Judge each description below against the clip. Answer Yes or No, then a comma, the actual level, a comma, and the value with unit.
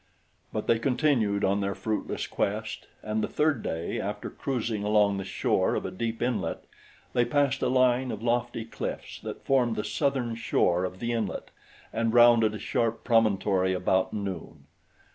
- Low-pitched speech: Yes, low, 115 Hz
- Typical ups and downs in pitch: Yes, average, 3.2 semitones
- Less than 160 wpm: No, average, 165 wpm